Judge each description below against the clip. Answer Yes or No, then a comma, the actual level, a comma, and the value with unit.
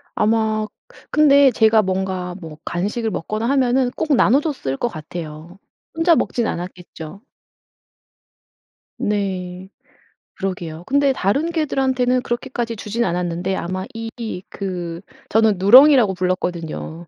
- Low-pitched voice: No, high, 205 Hz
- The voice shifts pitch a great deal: Yes, wide, 5.7 semitones